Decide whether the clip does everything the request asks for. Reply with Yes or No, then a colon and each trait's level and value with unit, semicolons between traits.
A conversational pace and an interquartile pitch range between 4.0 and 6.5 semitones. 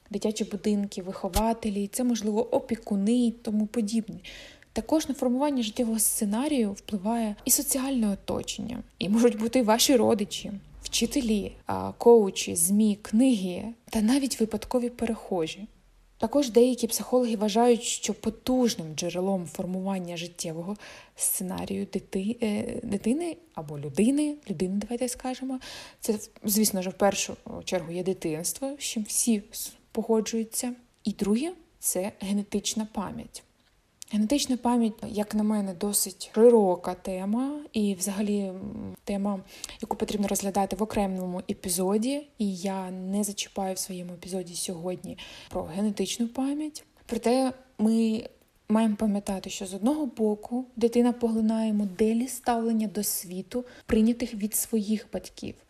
No: average, 120 wpm; average, 3.2 semitones